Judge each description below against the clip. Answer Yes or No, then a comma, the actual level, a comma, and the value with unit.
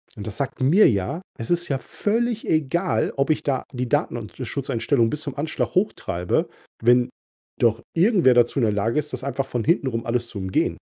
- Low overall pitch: Yes, low, 130 Hz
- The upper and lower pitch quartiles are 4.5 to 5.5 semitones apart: Yes, average, 5.1 semitones